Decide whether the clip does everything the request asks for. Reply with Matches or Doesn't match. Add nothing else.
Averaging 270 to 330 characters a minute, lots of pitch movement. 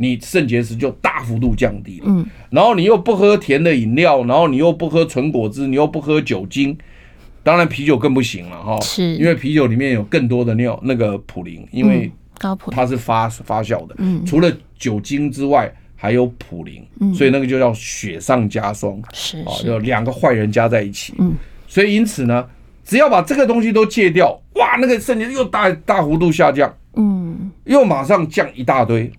Matches